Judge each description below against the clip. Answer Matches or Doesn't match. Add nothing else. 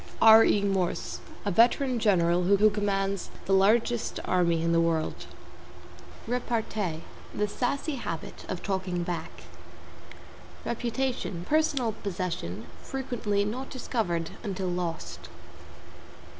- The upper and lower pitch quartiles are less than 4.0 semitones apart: Doesn't match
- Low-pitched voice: Doesn't match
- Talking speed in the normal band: Doesn't match